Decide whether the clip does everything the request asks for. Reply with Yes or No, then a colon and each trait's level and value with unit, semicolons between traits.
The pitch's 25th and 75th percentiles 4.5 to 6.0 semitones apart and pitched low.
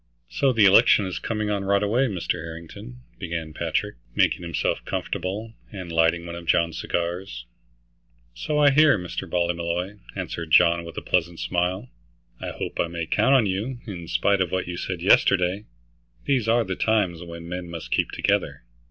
No: average, 3.7 semitones; very low, 90 Hz